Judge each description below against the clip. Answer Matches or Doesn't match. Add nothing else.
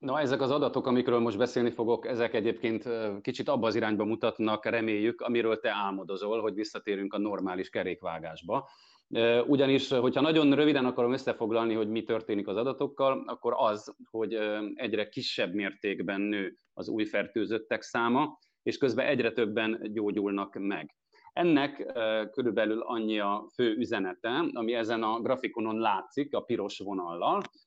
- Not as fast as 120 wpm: Doesn't match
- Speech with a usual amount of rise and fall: Doesn't match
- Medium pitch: Doesn't match